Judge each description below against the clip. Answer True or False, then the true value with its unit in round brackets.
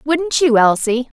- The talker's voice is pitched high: True (270 Hz)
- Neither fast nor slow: True (150 wpm)